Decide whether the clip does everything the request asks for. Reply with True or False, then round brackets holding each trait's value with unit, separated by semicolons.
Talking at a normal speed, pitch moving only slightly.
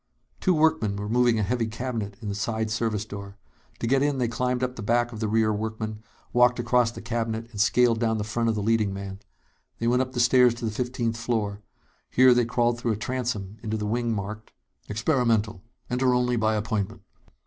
False (210 wpm; 2.3 semitones)